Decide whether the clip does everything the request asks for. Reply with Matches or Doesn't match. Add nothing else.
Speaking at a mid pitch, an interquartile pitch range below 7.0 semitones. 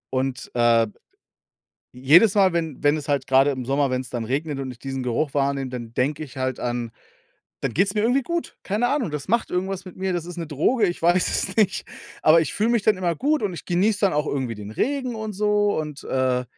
Doesn't match